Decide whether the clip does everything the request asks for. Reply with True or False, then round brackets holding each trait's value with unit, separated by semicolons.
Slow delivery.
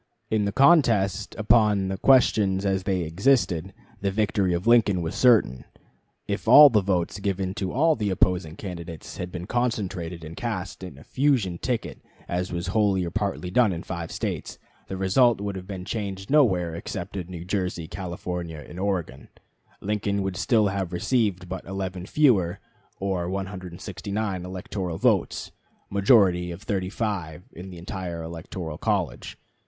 False (155 wpm)